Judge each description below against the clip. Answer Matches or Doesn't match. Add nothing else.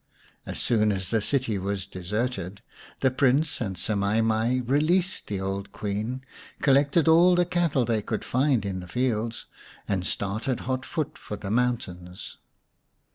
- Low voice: Matches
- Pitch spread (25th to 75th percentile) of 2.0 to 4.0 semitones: Doesn't match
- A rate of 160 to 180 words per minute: Doesn't match